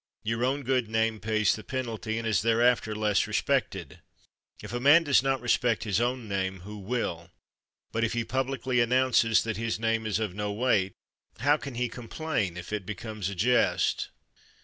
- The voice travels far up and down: No, average, 2.8 semitones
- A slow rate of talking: No, average, 180 wpm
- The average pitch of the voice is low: Yes, low, 115 Hz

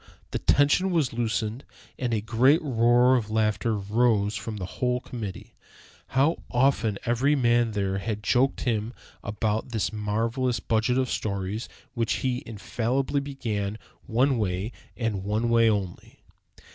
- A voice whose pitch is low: Yes, low, 115 Hz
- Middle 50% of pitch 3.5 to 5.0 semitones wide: No, average, 3.0 semitones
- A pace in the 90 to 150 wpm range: Yes, average, 140 wpm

